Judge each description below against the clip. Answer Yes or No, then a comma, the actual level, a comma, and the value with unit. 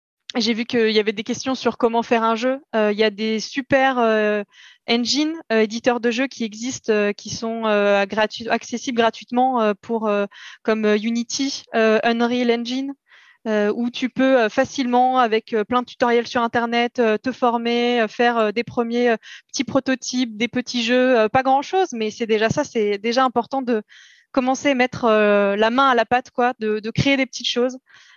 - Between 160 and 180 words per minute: No, average, 200 wpm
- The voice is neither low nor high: No, high, 235 Hz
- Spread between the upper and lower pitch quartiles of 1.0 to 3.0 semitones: Yes, narrow, 2.6 semitones